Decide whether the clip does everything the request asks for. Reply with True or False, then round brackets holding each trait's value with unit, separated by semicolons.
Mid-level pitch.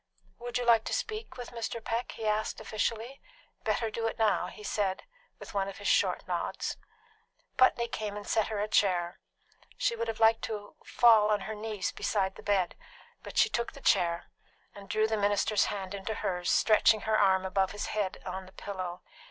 False (210 Hz)